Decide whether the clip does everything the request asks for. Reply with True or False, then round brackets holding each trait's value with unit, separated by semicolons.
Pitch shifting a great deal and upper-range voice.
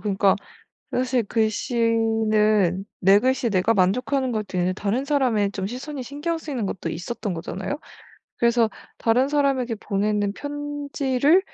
False (4.7 semitones; 230 Hz)